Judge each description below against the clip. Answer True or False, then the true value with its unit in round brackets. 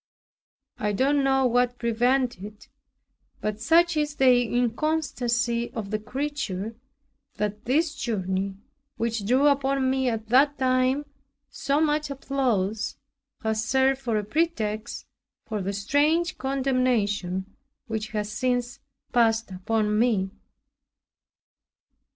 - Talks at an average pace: False (115 wpm)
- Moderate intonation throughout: True (4.2 semitones)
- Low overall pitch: False (245 Hz)